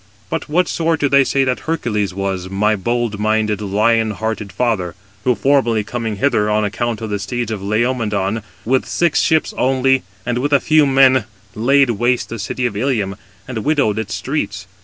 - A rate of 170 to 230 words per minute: Yes, average, 180 wpm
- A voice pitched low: Yes, low, 115 Hz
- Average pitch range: Yes, average, 4.0 semitones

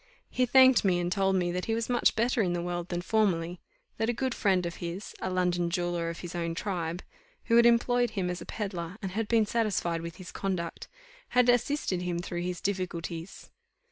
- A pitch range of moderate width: Yes, average, 4.2 semitones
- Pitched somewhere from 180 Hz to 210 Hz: Yes, medium, 185 Hz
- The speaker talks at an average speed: No, fast, 210 wpm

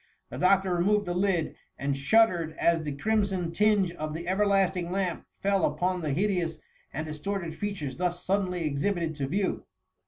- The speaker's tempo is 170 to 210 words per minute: No, average, 160 wpm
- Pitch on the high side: No, medium, 180 Hz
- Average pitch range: Yes, average, 3.6 semitones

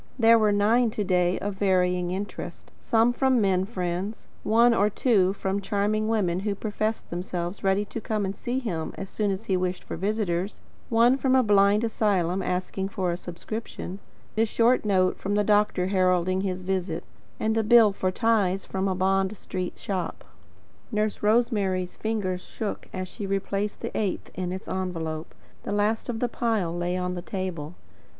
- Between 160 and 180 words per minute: Yes, average, 175 wpm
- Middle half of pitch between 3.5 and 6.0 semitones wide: No, average, 2.9 semitones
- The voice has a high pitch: Yes, high, 195 Hz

